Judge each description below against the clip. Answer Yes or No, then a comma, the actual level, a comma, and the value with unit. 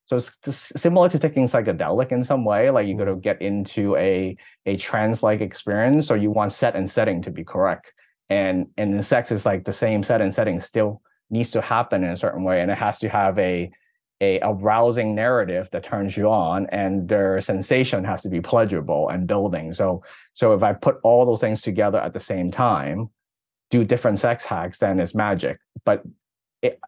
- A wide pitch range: No, average, 3.9 semitones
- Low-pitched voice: Yes, low, 110 Hz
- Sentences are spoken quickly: Yes, fast, 210 wpm